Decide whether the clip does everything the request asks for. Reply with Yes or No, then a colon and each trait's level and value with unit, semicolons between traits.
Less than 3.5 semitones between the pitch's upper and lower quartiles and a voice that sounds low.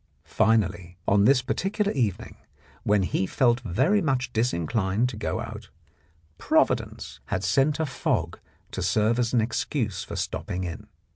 No: average, 4.6 semitones; low, 115 Hz